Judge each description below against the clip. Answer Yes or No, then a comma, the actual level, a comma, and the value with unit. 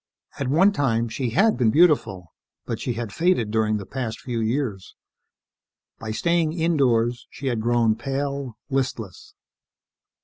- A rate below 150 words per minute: Yes, average, 140 wpm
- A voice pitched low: Yes, low, 120 Hz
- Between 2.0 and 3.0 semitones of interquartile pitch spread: No, average, 4.3 semitones